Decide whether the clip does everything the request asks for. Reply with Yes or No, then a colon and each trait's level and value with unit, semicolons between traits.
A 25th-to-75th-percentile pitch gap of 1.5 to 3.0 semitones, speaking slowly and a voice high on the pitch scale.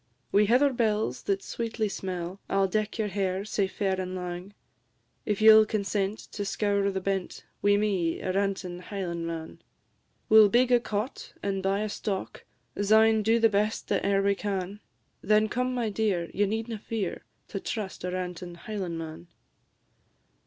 No: narrow, 2.4 semitones; average, 165 wpm; high, 200 Hz